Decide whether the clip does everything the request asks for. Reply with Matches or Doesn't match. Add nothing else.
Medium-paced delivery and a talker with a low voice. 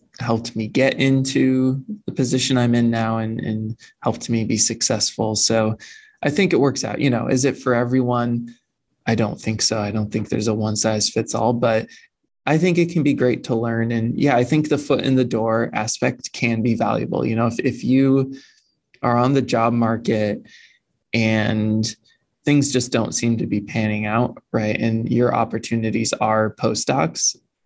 Matches